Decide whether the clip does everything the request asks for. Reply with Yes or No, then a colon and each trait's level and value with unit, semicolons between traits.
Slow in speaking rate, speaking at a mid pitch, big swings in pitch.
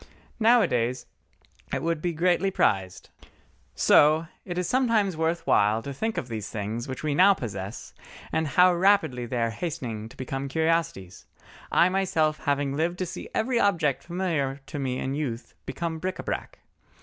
No: average, 160 wpm; medium, 155 Hz; wide, 6.3 semitones